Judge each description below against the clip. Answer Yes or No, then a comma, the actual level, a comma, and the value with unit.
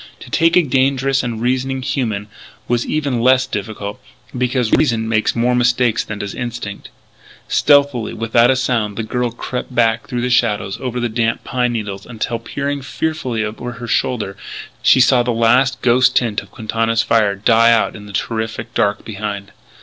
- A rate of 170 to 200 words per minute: Yes, average, 175 wpm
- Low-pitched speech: Yes, low, 120 Hz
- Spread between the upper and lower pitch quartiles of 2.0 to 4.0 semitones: Yes, narrow, 2.4 semitones